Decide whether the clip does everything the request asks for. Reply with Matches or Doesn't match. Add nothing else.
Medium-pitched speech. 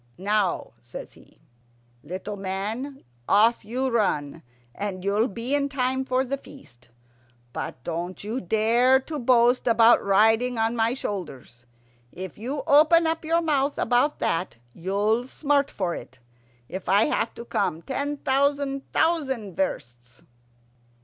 Doesn't match